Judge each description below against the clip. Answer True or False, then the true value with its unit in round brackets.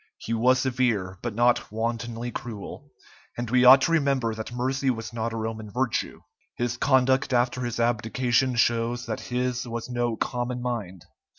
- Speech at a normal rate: True (165 wpm)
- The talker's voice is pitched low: True (120 Hz)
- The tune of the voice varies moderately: False (1.7 semitones)